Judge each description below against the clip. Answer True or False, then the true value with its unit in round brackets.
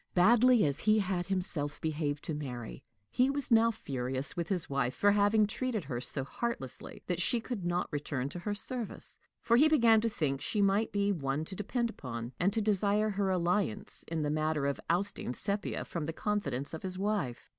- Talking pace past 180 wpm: True (200 wpm)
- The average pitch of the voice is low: False (185 Hz)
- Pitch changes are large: True (6.5 semitones)